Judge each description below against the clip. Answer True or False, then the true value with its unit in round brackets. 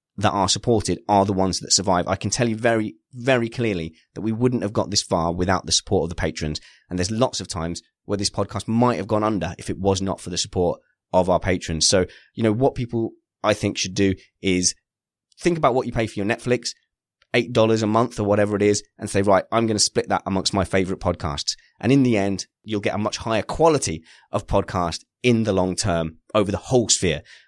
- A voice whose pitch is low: True (100 Hz)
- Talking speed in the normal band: False (235 wpm)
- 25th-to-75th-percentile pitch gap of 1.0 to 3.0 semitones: False (3.7 semitones)